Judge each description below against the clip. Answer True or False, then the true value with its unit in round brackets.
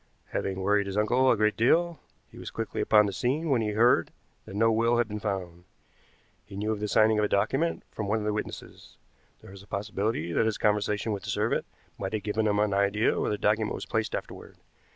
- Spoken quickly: True (230 wpm)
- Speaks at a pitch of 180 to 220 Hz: False (105 Hz)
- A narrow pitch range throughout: True (1.8 semitones)